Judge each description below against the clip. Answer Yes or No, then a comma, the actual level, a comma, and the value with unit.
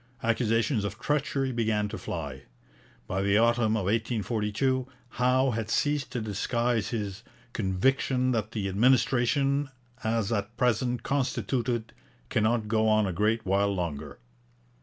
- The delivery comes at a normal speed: No, slow, 130 wpm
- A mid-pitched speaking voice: No, low, 115 Hz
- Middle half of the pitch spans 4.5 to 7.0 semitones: No, average, 3.2 semitones